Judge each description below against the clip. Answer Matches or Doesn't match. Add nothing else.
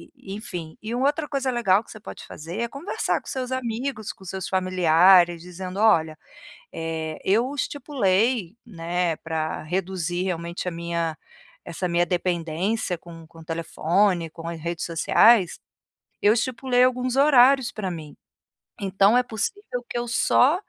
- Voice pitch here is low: Doesn't match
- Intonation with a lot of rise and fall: Matches